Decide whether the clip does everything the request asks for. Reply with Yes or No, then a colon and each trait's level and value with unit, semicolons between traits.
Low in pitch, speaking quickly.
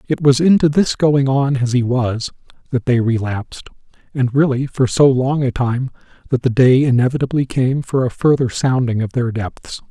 No: low, 130 Hz; average, 190 wpm